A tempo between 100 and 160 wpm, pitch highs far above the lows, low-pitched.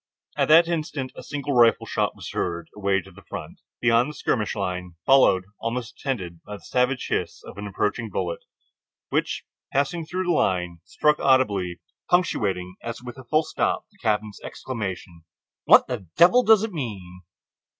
No: average, 170 wpm; wide, 6.8 semitones; low, 115 Hz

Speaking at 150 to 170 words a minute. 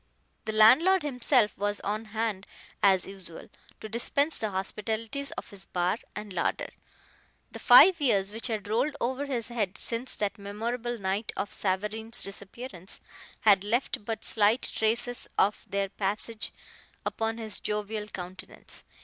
No: average, 140 wpm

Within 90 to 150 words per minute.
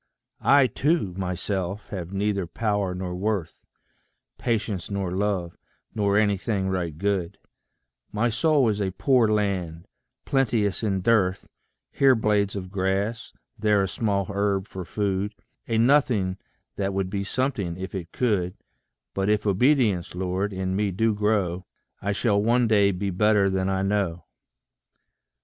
Yes: average, 140 wpm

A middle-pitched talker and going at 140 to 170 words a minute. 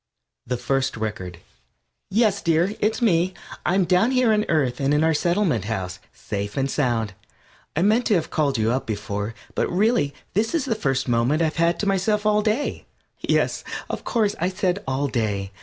No: medium, 160 Hz; average, 190 wpm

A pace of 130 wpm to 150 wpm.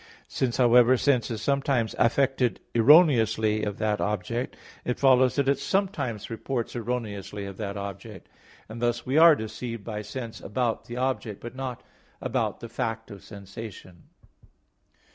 Yes: average, 145 wpm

